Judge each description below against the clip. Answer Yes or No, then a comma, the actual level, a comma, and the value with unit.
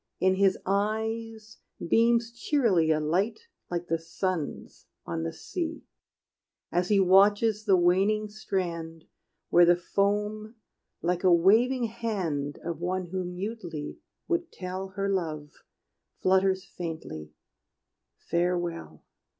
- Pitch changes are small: No, average, 3.8 semitones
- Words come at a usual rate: No, slow, 115 wpm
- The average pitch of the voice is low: No, high, 190 Hz